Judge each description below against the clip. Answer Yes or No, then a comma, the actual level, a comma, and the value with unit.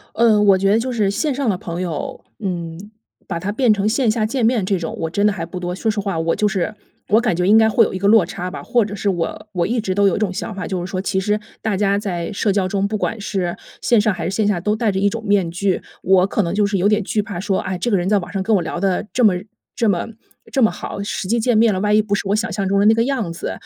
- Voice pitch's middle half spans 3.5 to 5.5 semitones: No, average, 2.8 semitones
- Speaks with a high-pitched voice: Yes, high, 200 Hz